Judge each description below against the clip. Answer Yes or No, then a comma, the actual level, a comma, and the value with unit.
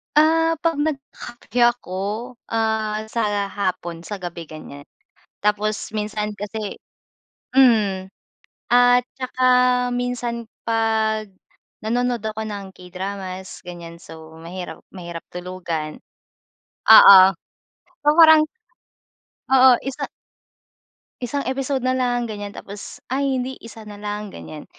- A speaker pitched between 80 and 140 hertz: No, high, 215 Hz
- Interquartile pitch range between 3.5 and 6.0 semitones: Yes, average, 4.7 semitones